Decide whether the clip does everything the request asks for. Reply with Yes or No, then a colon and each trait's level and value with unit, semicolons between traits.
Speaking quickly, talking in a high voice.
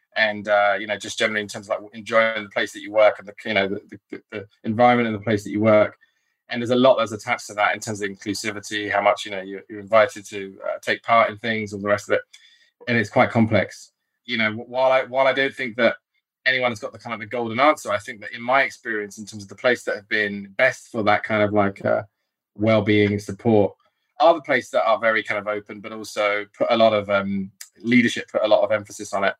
No: fast, 265 wpm; low, 110 Hz